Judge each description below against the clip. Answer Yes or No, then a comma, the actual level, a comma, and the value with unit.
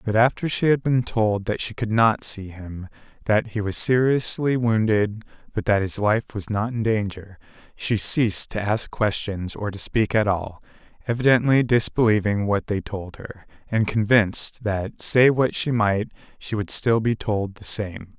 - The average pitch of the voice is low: Yes, low, 110 Hz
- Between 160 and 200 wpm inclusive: Yes, average, 180 wpm